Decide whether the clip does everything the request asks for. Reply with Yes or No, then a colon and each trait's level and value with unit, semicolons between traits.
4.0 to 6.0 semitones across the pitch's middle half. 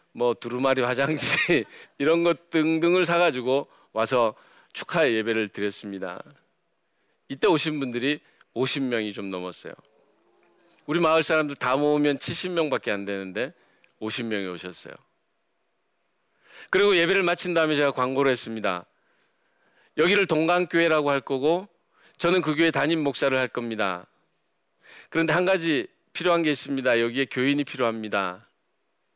Yes: wide, 5.6 semitones